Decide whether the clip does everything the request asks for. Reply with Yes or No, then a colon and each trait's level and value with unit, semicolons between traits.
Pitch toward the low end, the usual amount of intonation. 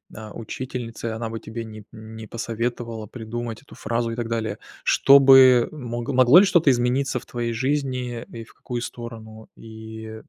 No: low, 115 Hz; narrow, 2.2 semitones